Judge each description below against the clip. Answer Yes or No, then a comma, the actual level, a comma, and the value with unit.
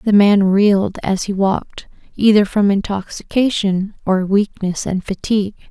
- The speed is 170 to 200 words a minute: No, slow, 135 wpm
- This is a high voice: Yes, high, 200 Hz